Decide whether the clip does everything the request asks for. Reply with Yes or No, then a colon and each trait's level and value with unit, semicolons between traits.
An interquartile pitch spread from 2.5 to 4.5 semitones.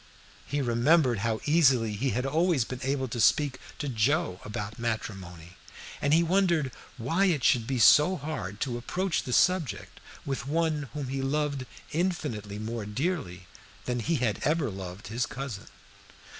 No: wide, 5.5 semitones